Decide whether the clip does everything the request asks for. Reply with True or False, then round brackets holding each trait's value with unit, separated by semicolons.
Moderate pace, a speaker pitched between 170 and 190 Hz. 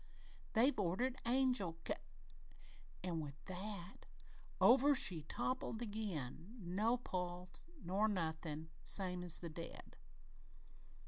False (110 wpm; 185 Hz)